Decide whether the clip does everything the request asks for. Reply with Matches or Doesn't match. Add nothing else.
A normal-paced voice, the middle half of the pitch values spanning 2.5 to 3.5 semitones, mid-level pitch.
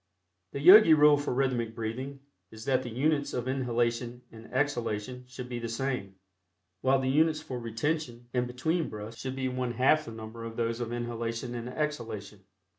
Doesn't match